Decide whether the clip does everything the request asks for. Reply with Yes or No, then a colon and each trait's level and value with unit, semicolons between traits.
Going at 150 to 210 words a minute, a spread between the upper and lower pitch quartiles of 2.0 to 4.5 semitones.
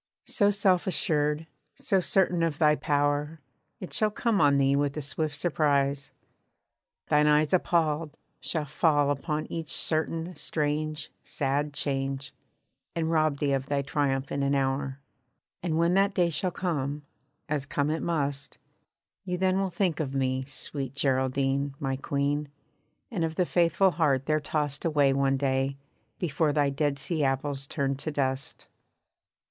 Yes: average, 155 wpm; average, 2.8 semitones